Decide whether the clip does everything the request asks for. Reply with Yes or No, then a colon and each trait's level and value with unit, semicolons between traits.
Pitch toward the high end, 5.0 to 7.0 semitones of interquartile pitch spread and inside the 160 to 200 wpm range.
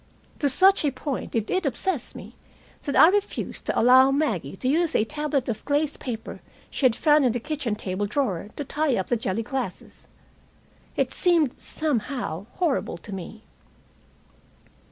Yes: very high, 265 Hz; wide, 5.4 semitones; average, 165 wpm